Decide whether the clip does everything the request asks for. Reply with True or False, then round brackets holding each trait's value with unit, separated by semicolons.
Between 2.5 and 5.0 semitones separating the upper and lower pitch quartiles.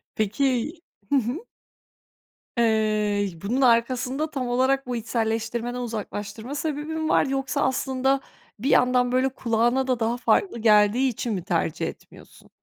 True (3.2 semitones)